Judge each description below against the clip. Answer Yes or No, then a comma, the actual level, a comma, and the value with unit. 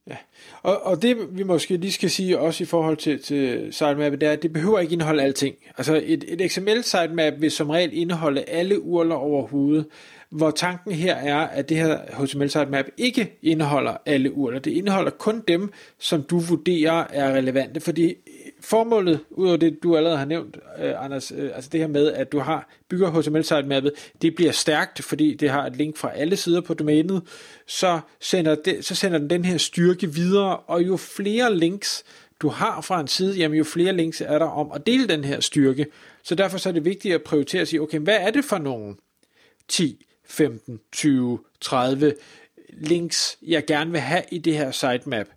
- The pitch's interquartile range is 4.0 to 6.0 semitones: No, average, 3.6 semitones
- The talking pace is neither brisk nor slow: Yes, average, 195 wpm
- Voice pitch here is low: No, medium, 160 Hz